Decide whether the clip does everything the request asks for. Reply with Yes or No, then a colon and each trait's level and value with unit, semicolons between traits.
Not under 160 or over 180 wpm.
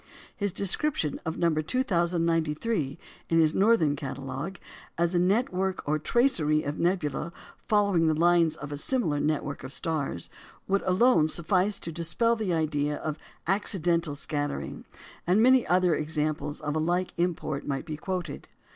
No: average, 145 wpm